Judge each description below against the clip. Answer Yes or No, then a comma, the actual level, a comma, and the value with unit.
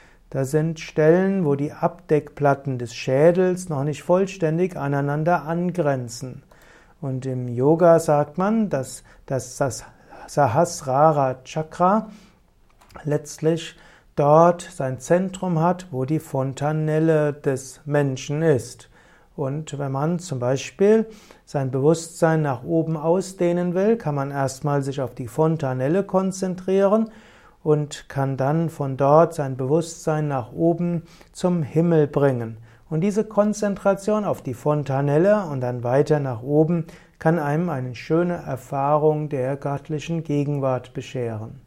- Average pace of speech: No, slow, 120 wpm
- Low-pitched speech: No, medium, 150 Hz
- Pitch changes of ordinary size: Yes, average, 3.9 semitones